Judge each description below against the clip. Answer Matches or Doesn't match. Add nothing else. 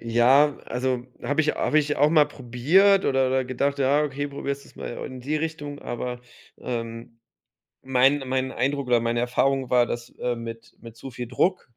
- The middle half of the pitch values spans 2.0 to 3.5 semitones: Matches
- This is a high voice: Doesn't match